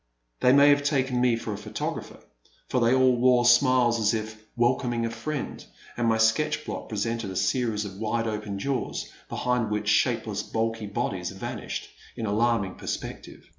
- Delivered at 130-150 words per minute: No, average, 175 wpm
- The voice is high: No, low, 115 Hz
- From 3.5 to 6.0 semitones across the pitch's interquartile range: No, average, 2.7 semitones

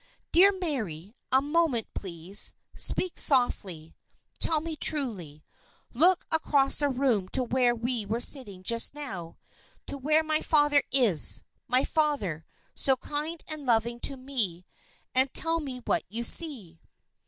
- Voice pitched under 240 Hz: No, very high, 260 Hz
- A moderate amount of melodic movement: No, wide, 6.3 semitones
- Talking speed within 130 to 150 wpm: Yes, average, 140 wpm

